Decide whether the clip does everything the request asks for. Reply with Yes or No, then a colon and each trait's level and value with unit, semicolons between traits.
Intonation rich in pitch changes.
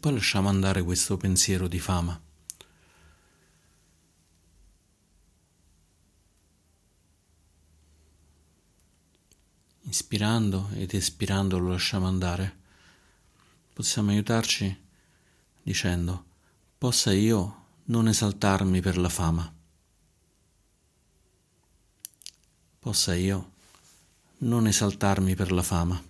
No: average, 2.9 semitones